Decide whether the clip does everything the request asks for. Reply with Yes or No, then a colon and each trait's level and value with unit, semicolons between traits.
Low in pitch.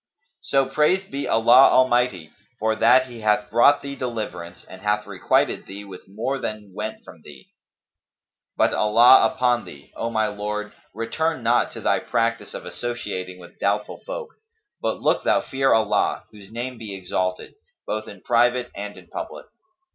Yes: low, 115 Hz